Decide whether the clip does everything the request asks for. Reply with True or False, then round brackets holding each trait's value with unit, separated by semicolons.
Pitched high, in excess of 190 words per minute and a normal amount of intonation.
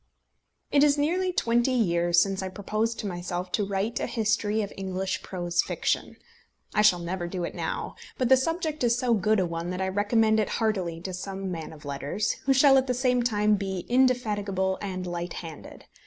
True (205 Hz; 200 wpm; 4.6 semitones)